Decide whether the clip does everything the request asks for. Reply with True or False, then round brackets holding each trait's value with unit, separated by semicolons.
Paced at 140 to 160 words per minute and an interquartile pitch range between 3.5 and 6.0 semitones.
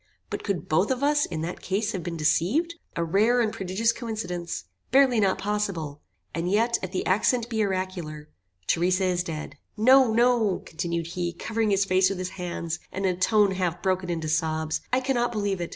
False (195 wpm; 4.3 semitones)